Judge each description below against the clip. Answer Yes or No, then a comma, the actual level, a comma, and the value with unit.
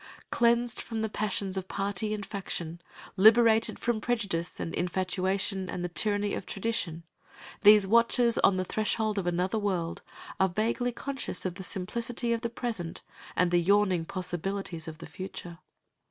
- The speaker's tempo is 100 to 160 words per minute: Yes, average, 155 wpm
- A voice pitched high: Yes, high, 200 Hz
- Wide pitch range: No, average, 3.6 semitones